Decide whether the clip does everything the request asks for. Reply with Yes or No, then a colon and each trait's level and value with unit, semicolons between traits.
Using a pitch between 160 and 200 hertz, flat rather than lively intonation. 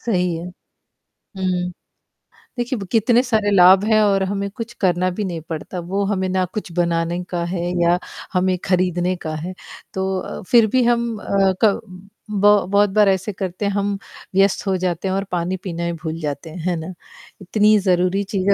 Yes: high, 190 Hz; narrow, 2.2 semitones